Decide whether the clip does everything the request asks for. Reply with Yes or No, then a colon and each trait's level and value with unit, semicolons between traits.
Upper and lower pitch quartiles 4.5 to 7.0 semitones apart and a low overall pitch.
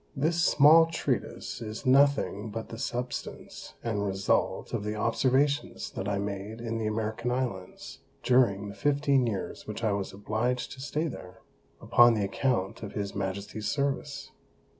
Yes: average, 5.0 semitones; low, 115 Hz